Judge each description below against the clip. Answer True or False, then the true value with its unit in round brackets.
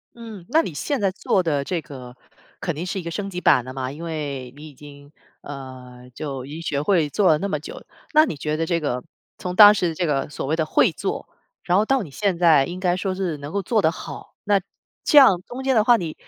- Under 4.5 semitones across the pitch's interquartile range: False (5.3 semitones)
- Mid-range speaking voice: True (165 Hz)